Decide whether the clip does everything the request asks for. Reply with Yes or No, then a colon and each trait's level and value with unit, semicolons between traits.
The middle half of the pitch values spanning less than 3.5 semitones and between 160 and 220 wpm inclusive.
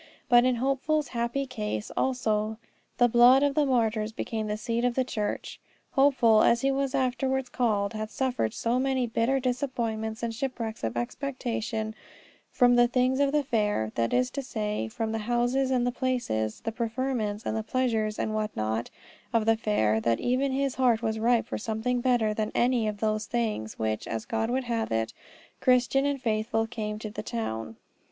Yes: average, 3.0 semitones; average, 180 wpm